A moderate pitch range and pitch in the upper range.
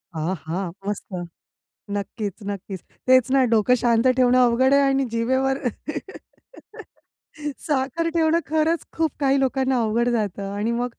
Yes: average, 4.3 semitones; very high, 250 Hz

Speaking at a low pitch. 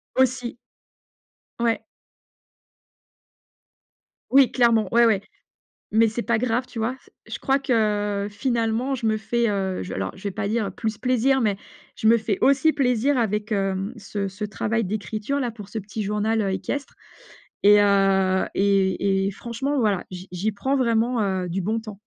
No: high, 220 Hz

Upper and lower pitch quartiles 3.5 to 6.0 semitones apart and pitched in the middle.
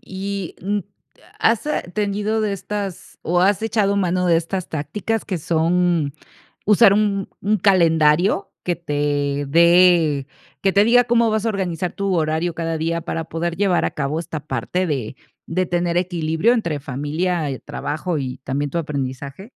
Yes: average, 4.2 semitones; medium, 175 Hz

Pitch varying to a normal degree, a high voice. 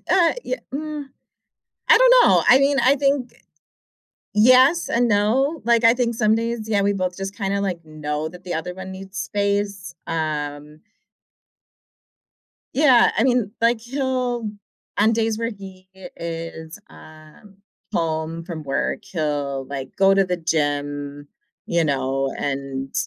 No: wide, 6.9 semitones; high, 195 Hz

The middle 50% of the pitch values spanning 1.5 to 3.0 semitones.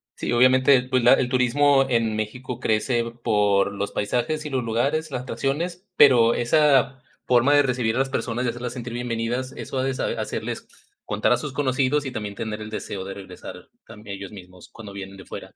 No: average, 3.5 semitones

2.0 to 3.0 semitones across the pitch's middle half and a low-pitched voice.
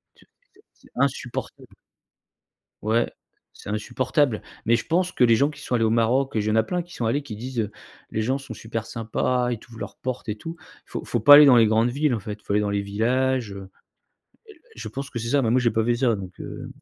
No: average, 3.4 semitones; low, 120 Hz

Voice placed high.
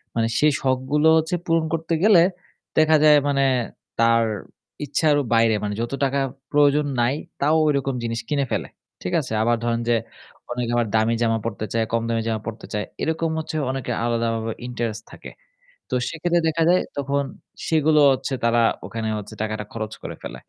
No: low, 125 Hz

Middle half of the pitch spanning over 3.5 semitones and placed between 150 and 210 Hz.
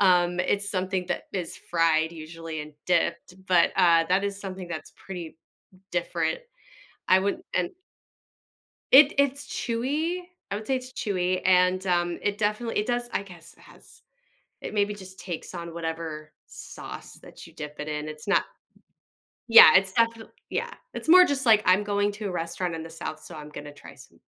Yes: average, 3.9 semitones; medium, 185 Hz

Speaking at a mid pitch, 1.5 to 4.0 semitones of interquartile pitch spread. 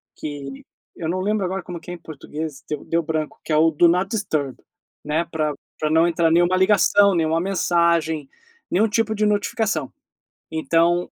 Yes: medium, 170 Hz; average, 3.1 semitones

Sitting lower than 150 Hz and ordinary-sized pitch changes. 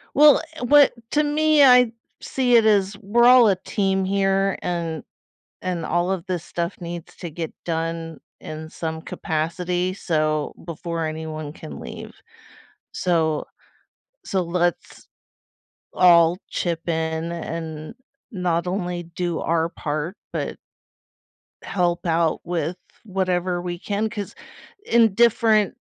No: medium, 175 Hz; average, 3.2 semitones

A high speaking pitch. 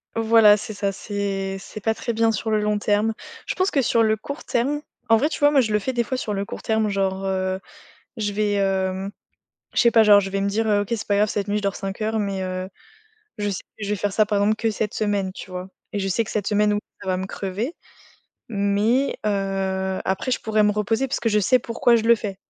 Yes: high, 210 Hz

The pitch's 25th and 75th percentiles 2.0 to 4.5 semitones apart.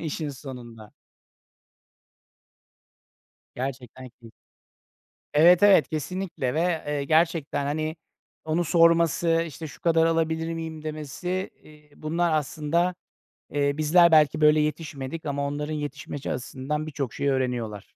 Yes: average, 2.7 semitones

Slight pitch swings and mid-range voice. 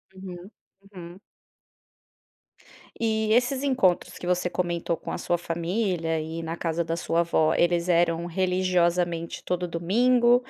Yes: narrow, 1.9 semitones; medium, 175 Hz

